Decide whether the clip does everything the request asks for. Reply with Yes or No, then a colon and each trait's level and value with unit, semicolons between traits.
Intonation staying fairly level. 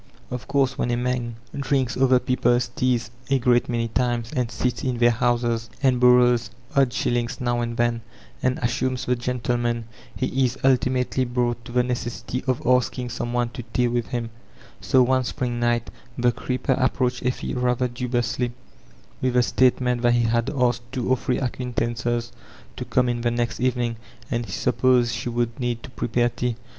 Yes: narrow, 1.0 semitones